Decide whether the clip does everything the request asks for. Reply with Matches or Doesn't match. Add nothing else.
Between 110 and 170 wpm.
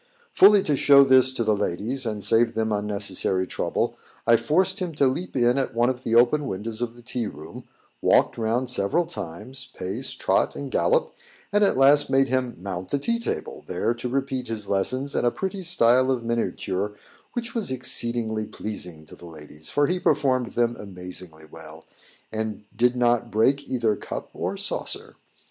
Doesn't match